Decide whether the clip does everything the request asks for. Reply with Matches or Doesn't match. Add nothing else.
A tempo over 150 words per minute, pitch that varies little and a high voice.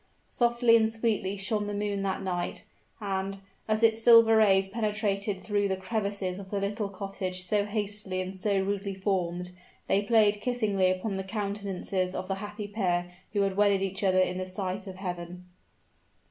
Matches